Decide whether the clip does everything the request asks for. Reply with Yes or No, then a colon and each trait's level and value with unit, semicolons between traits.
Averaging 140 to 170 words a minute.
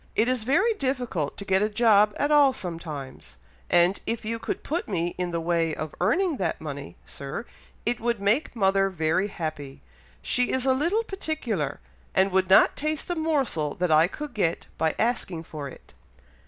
No: average, 180 wpm